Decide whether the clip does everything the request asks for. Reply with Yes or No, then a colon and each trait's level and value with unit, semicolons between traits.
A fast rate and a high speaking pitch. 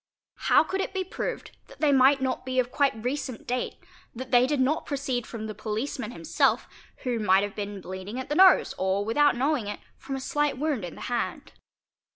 Yes: fast, 210 wpm; very high, 255 Hz